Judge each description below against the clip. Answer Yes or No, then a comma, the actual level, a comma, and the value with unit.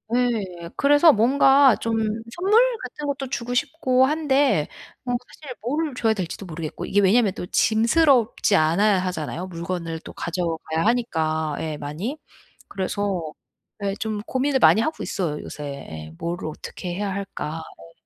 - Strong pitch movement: Yes, wide, 7.5 semitones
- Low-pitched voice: No, high, 205 Hz